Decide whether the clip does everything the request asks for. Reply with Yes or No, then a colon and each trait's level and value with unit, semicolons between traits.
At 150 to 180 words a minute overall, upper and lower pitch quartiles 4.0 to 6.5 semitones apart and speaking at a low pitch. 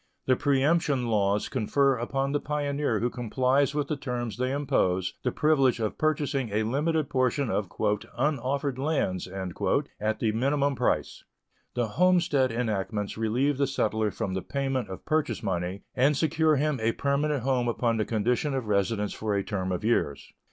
Yes: average, 165 wpm; average, 4.6 semitones; low, 125 Hz